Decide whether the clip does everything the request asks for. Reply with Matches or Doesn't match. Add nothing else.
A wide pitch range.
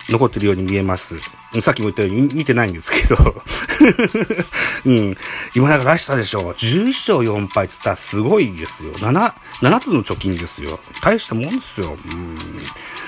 Matches